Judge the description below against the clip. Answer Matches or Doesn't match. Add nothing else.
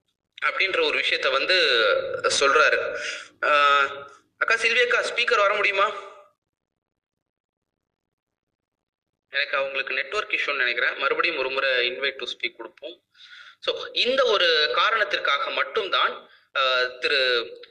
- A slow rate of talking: Doesn't match